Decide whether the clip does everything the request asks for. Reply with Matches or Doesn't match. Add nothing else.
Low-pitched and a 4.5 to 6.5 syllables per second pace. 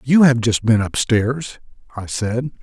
Doesn't match